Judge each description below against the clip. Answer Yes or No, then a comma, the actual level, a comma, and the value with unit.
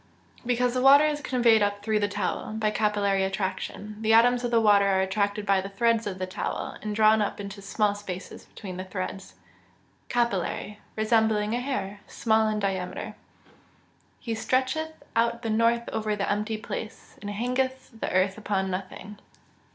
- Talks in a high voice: Yes, high, 215 Hz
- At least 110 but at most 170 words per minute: No, average, 180 wpm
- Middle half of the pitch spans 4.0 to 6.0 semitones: No, narrow, 2.6 semitones